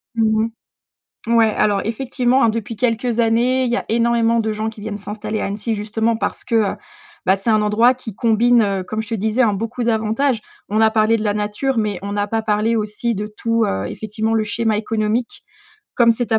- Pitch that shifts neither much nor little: No, narrow, 1.6 semitones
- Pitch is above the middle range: Yes, high, 220 Hz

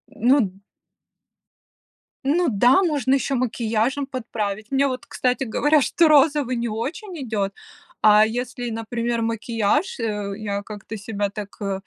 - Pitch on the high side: Yes, high, 235 Hz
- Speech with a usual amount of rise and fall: Yes, average, 4.1 semitones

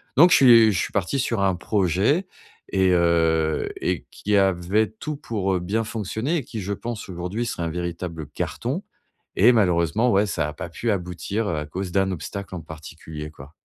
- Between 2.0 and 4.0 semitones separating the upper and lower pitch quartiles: No, average, 4.6 semitones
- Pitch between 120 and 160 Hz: No, very low, 95 Hz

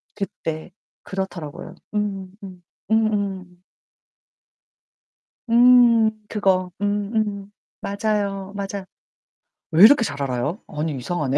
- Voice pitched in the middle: No, high, 195 Hz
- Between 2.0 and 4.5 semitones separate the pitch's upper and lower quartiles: Yes, average, 3.0 semitones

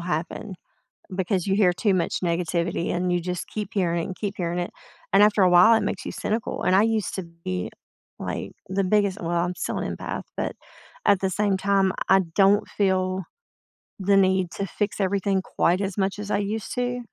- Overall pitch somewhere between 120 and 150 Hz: No, high, 190 Hz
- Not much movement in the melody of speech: Yes, narrow, 2.2 semitones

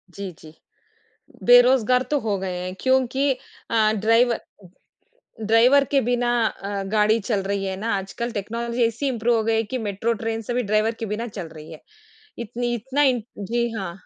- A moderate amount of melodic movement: Yes, average, 3.2 semitones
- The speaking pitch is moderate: No, high, 225 Hz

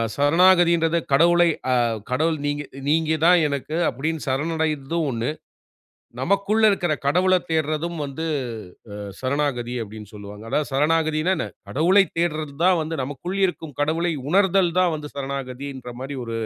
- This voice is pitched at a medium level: Yes, medium, 155 Hz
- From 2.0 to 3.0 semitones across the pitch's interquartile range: No, average, 3.7 semitones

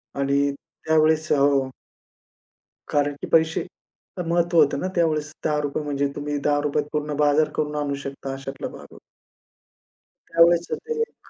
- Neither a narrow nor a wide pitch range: No, narrow, 2.0 semitones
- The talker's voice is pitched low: No, medium, 150 Hz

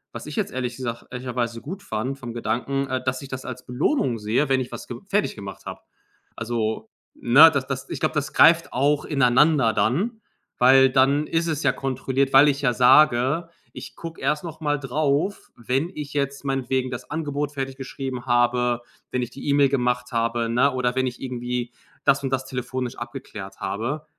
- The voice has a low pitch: Yes, low, 130 Hz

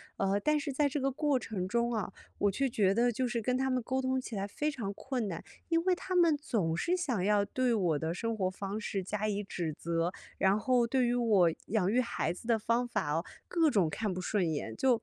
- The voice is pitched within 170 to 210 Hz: No, high, 225 Hz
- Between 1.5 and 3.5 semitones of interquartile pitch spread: No, average, 5.0 semitones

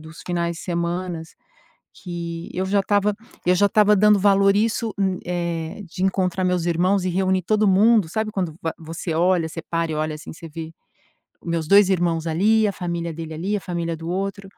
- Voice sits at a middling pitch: Yes, medium, 180 Hz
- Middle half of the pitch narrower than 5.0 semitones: Yes, average, 2.9 semitones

